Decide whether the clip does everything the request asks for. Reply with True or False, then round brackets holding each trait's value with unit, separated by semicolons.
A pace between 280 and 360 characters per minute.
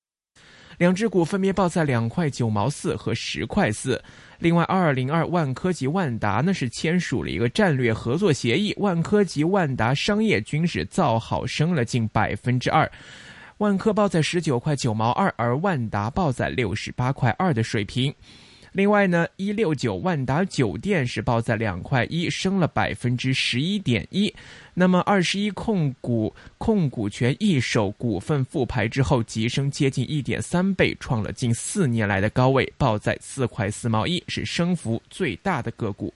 False (260 characters per minute)